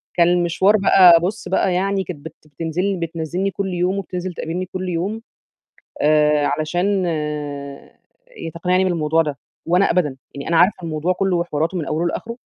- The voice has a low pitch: No, medium, 175 Hz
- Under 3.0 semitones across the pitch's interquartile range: Yes, narrow, 2.6 semitones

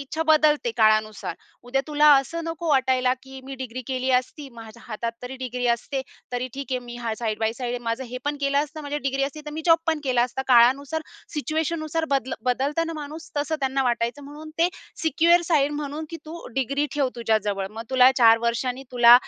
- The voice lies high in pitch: Yes, very high, 265 Hz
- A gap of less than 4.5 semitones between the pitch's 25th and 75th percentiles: Yes, average, 3.6 semitones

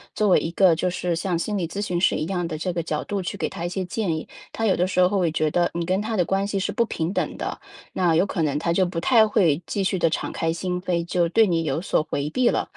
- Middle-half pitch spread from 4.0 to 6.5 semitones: No, average, 2.7 semitones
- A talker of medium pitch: Yes, medium, 180 Hz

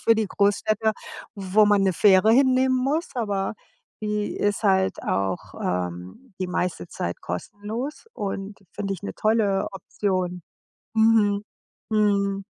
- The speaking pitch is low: No, high, 205 Hz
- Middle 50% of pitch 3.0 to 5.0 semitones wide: No, narrow, 2.6 semitones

